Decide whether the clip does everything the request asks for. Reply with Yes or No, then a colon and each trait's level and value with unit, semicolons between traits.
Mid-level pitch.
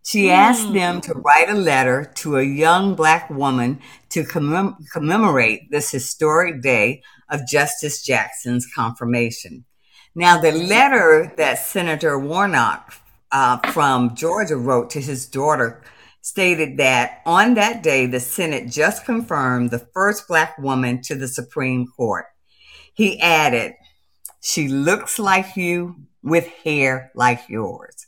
Yes: medium, 150 Hz